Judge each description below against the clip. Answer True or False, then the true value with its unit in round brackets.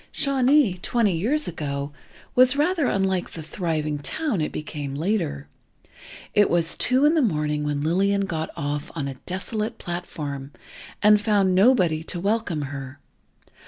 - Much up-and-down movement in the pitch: True (6.5 semitones)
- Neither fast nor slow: True (145 wpm)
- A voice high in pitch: False (180 Hz)